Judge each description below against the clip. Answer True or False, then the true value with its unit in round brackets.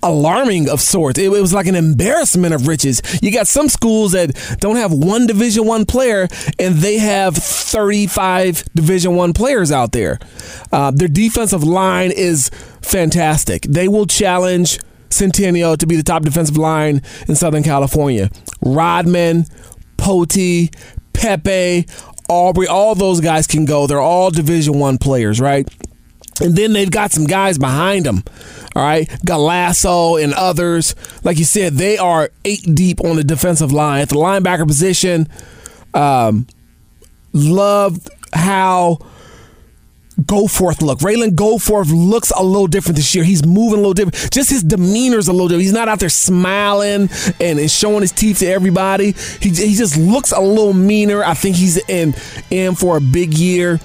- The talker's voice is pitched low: False (180 Hz)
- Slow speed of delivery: False (160 wpm)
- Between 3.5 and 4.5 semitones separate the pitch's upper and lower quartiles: True (4.0 semitones)